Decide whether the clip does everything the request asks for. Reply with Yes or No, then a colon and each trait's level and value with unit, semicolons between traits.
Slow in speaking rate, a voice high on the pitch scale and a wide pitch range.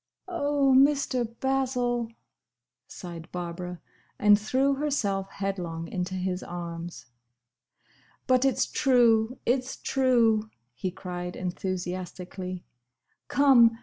Yes: slow, 90 wpm; high, 210 Hz; wide, 6.2 semitones